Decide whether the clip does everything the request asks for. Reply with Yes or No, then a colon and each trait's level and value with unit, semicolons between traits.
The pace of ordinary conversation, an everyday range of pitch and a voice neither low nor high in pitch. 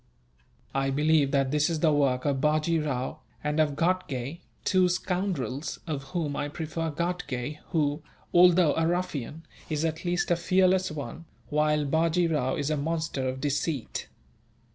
Yes: average, 155 wpm; average, 3.0 semitones; medium, 155 Hz